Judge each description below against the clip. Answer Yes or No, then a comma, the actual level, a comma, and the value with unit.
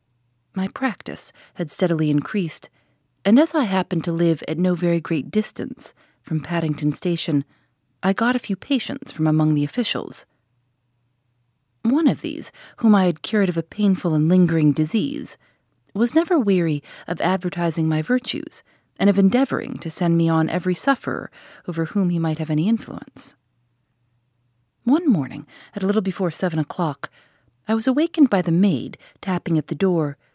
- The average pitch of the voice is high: No, medium, 170 Hz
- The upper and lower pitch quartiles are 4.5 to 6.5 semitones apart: Yes, wide, 5.5 semitones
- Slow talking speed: No, average, 160 wpm